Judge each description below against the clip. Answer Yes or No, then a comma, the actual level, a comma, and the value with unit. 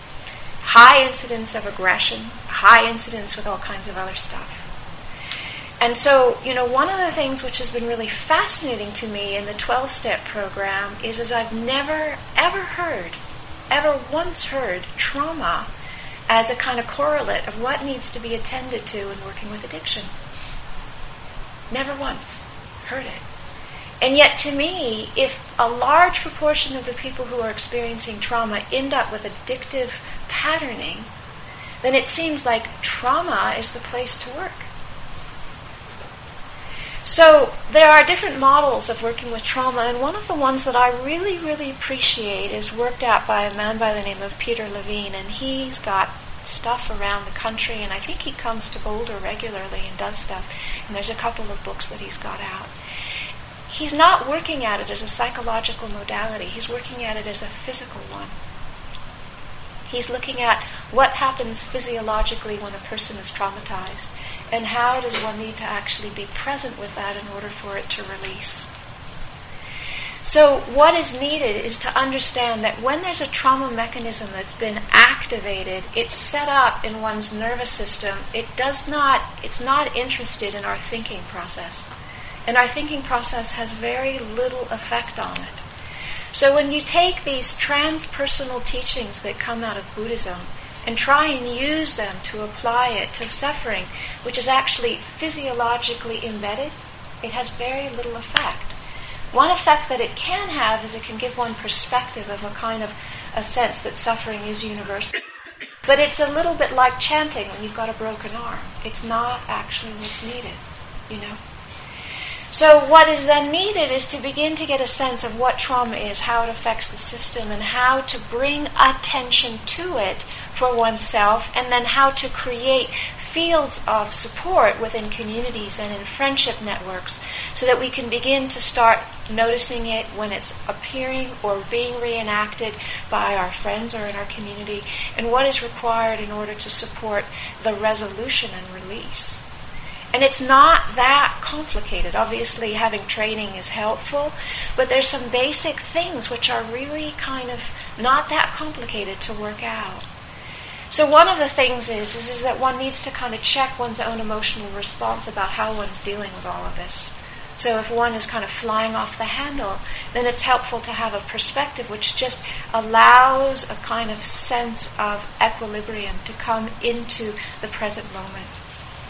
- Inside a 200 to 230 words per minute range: No, average, 170 wpm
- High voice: Yes, high, 245 Hz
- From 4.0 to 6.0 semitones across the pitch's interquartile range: No, average, 3.6 semitones